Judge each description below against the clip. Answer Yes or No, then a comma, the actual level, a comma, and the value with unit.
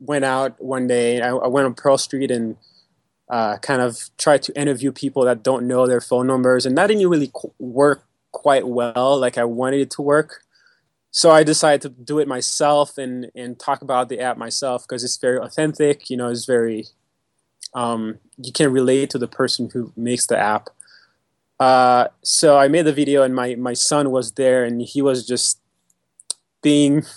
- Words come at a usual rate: Yes, average, 195 wpm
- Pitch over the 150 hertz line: No, low, 130 Hz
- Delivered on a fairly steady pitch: Yes, narrow, 2.3 semitones